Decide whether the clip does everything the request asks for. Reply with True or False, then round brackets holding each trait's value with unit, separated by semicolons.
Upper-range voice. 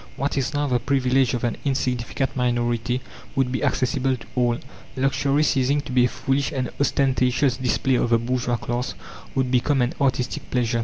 False (130 Hz)